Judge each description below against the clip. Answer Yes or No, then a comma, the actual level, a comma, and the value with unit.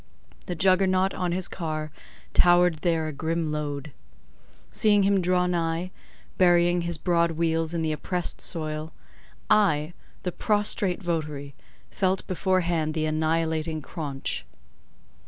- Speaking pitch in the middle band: Yes, medium, 170 Hz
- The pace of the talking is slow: Yes, slow, 115 wpm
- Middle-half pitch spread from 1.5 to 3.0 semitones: Yes, narrow, 2.6 semitones